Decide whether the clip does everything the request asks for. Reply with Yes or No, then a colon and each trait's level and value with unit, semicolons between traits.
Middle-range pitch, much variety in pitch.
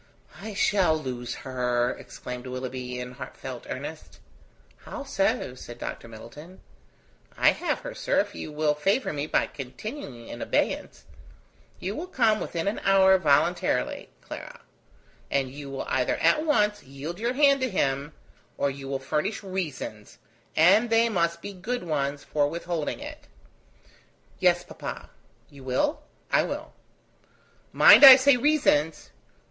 Yes: medium, 155 Hz; wide, 7.9 semitones